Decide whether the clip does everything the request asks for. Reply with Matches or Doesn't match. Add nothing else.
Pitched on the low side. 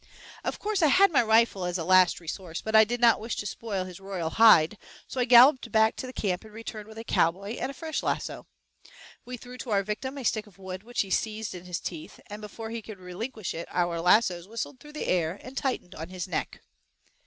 Doesn't match